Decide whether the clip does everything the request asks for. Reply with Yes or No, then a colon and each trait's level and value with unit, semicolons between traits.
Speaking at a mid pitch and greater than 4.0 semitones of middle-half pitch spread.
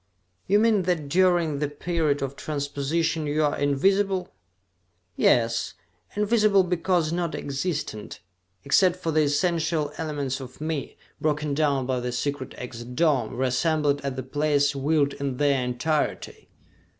No: medium, 150 Hz; average, 3.5 semitones